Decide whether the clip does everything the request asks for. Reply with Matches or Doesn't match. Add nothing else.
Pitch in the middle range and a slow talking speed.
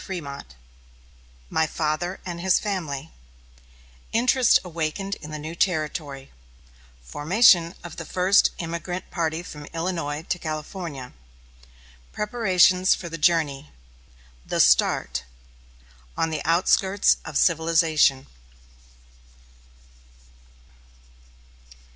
Matches